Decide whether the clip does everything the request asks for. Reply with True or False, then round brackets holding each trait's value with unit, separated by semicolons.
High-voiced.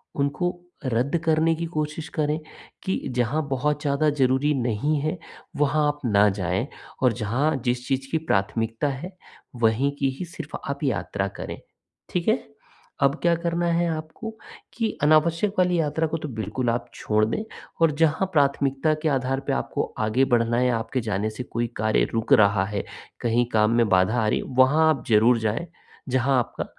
False (135 Hz)